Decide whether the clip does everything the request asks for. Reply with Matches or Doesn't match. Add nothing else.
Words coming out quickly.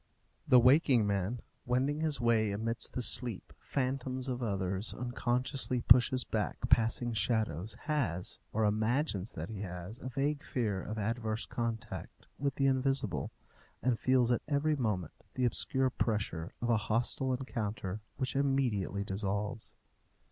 Doesn't match